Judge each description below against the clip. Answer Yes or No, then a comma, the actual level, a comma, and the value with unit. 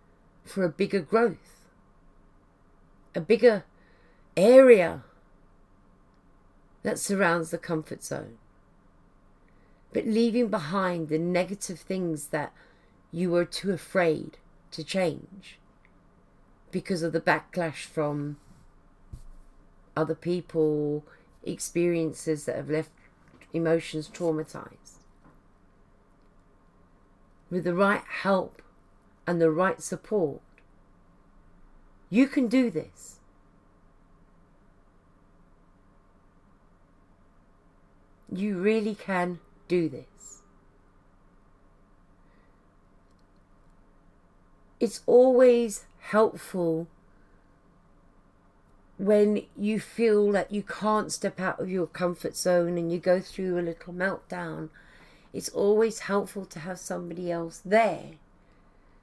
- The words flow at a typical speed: No, slow, 85 wpm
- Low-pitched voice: No, medium, 155 Hz